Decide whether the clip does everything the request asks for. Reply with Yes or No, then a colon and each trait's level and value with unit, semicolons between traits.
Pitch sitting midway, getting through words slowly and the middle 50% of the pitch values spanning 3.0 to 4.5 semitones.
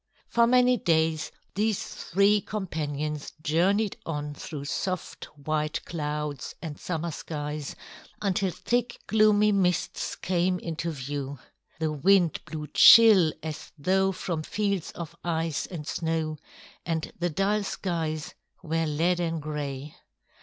Yes: medium, 165 Hz; slow, 120 wpm; average, 4.0 semitones